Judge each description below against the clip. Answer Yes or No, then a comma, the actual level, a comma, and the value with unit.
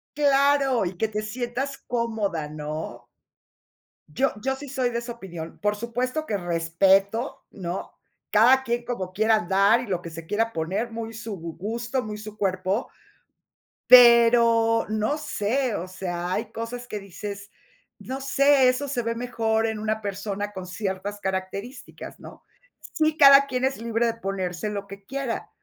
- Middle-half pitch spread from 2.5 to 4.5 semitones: Yes, average, 4.1 semitones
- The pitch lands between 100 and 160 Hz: No, high, 220 Hz